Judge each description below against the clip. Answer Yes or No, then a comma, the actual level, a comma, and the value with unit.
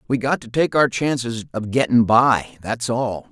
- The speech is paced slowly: No, average, 200 wpm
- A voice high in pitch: No, low, 120 Hz